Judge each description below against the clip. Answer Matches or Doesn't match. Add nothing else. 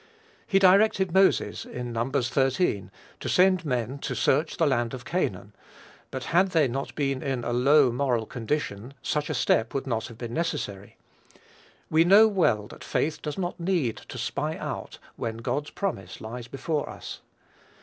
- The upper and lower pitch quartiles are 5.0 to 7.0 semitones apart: Matches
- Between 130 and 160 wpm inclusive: Doesn't match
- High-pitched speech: Doesn't match